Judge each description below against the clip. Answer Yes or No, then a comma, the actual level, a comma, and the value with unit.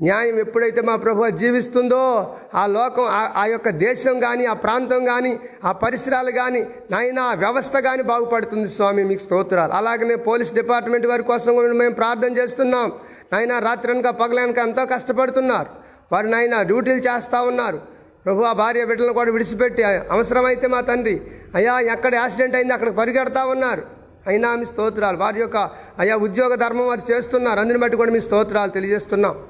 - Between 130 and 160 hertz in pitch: No, high, 240 Hz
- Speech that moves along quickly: Yes, fast, 155 wpm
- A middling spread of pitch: No, narrow, 1.8 semitones